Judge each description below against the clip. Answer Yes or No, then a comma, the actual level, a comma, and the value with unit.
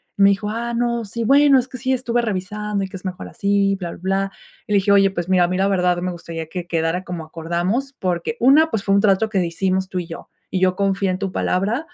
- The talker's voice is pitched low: No, high, 195 Hz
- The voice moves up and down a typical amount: Yes, average, 3.4 semitones